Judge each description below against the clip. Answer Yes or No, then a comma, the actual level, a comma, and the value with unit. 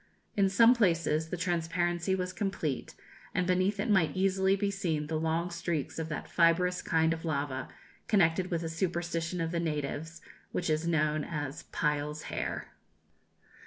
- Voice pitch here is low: No, medium, 170 Hz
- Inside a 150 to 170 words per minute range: Yes, average, 160 wpm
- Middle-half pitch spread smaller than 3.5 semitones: Yes, narrow, 2.5 semitones